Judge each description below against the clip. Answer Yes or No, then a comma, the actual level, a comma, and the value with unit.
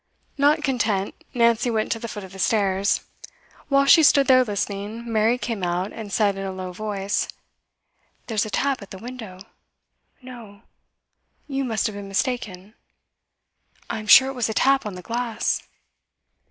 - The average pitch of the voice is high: Yes, high, 220 Hz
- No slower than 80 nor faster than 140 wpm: No, average, 165 wpm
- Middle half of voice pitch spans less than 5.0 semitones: Yes, average, 3.9 semitones